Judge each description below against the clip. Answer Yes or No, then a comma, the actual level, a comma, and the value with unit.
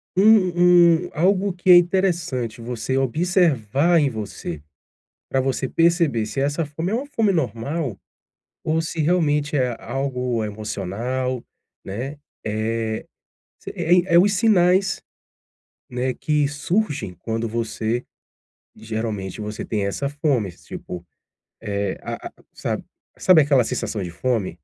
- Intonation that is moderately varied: No, wide, 7.3 semitones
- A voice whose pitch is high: No, low, 135 Hz